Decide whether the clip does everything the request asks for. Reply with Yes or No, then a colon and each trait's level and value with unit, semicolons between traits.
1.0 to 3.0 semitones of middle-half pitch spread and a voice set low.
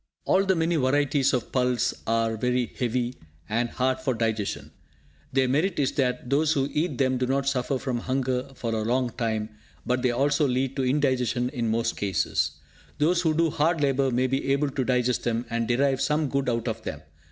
Yes: narrow, 2.6 semitones; low, 130 Hz